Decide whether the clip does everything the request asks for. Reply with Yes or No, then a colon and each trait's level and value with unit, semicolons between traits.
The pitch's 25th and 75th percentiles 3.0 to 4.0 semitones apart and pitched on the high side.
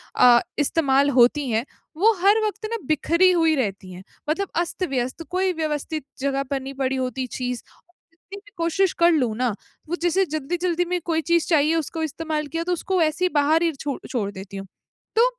No: average, 4.7 semitones; very high, 310 Hz